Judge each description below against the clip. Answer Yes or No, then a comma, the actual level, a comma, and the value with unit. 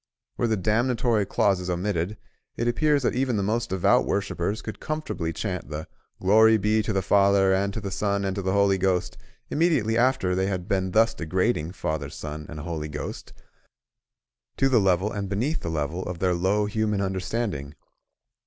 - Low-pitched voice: Yes, low, 100 Hz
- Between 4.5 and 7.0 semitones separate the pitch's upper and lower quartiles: No, average, 3.3 semitones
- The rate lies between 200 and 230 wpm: No, average, 180 wpm